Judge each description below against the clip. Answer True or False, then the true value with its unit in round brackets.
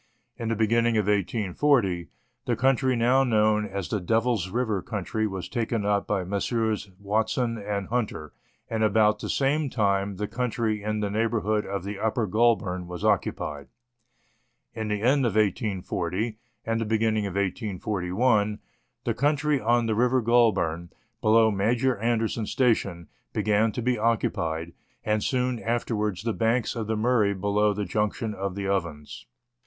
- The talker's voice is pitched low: True (110 Hz)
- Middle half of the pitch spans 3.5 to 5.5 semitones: False (2.7 semitones)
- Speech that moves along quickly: False (155 wpm)